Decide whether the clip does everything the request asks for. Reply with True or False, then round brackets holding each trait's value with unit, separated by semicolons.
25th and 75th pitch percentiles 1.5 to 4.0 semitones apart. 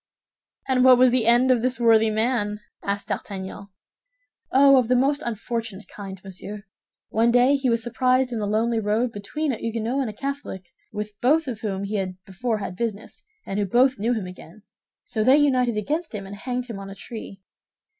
True (3.7 semitones)